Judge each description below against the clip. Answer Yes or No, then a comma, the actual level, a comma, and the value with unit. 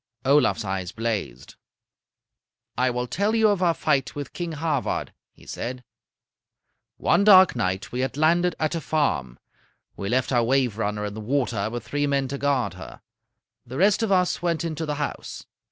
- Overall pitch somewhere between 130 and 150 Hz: Yes, medium, 140 Hz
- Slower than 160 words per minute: No, average, 170 wpm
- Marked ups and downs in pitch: Yes, wide, 5.9 semitones